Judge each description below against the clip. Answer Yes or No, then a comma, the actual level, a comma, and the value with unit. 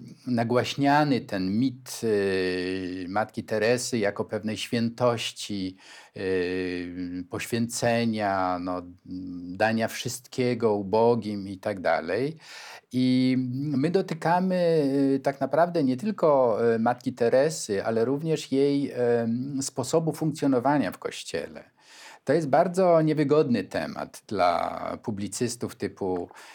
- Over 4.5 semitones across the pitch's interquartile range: Yes, wide, 5.5 semitones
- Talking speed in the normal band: No, slow, 90 wpm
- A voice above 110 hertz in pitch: Yes, low, 120 Hz